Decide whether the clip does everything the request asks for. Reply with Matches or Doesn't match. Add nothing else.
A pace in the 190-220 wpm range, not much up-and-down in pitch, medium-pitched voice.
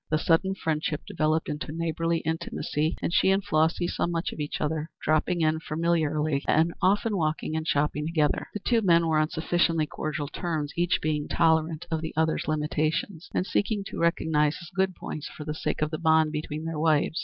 Matches